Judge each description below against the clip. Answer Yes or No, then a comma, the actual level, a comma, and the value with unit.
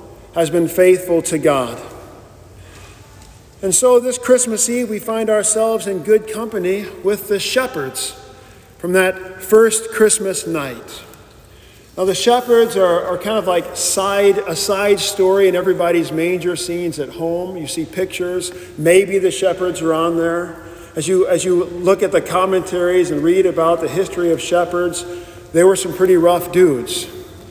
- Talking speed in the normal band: Yes, average, 155 wpm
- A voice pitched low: No, medium, 185 Hz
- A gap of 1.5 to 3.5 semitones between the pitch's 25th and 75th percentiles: Yes, average, 2.8 semitones